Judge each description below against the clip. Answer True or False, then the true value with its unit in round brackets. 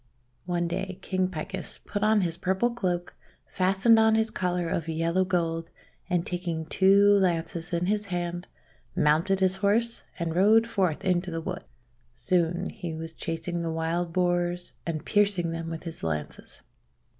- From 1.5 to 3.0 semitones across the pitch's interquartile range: True (2.5 semitones)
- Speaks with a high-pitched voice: False (175 Hz)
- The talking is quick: False (155 wpm)